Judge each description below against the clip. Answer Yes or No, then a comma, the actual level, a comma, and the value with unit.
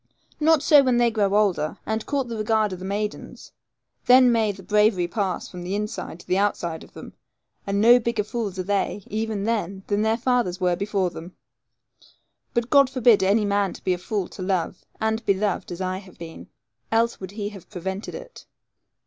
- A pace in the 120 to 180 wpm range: No, average, 200 wpm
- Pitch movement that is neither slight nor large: Yes, average, 3.2 semitones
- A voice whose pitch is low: No, high, 205 Hz